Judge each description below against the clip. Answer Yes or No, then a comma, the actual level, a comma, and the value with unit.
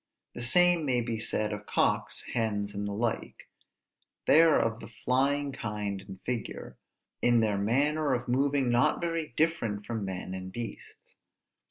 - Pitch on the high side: No, low, 120 Hz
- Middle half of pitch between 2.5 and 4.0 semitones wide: No, wide, 5.4 semitones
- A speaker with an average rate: Yes, average, 160 wpm